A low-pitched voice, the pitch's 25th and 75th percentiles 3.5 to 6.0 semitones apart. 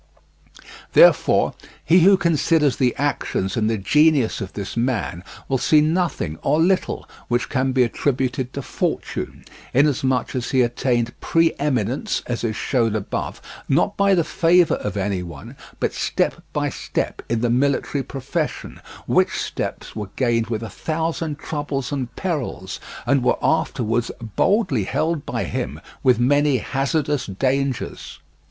Yes: low, 130 Hz; average, 4.5 semitones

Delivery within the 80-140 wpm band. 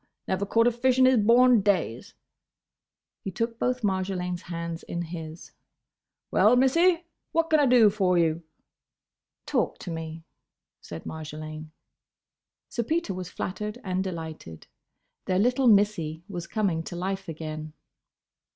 Yes: slow, 135 wpm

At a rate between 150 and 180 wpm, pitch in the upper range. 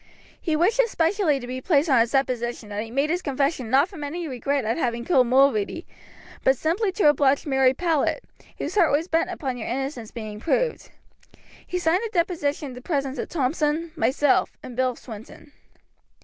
No: average, 190 wpm; very high, 280 Hz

